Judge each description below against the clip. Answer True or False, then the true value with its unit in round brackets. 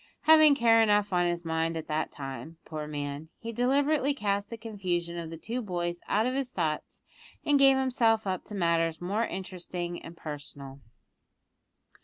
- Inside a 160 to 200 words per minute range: True (170 wpm)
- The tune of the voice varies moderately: False (5.9 semitones)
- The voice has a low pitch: False (185 Hz)